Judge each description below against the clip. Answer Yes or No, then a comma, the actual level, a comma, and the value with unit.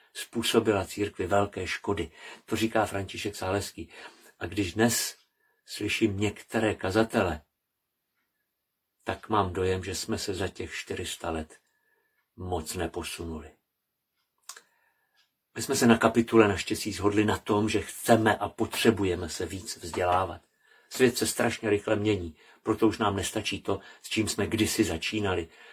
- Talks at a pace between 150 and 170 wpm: No, average, 135 wpm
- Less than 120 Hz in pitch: Yes, low, 105 Hz